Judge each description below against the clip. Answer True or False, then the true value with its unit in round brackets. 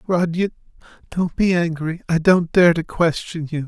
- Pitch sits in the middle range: True (170 Hz)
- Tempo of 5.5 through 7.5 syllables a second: False (4.6 syllables/s)